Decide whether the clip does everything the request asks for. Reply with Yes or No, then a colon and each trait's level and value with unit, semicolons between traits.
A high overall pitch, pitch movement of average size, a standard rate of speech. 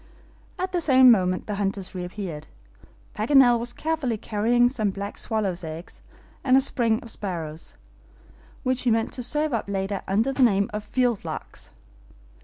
Yes: high, 220 Hz; average, 4.6 semitones; average, 160 wpm